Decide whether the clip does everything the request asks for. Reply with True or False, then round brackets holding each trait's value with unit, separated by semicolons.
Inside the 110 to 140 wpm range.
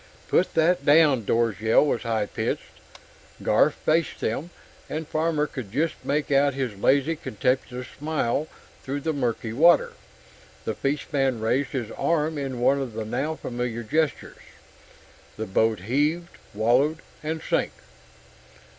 True (135 wpm)